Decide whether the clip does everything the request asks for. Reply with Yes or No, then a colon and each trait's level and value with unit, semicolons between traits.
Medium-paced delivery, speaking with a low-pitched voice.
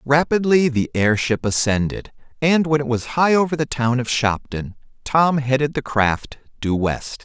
Yes: average, 165 wpm; low, 130 Hz